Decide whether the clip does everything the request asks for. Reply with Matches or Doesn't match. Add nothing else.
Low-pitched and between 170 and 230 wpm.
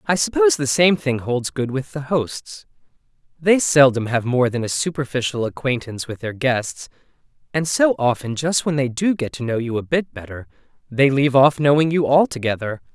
Matches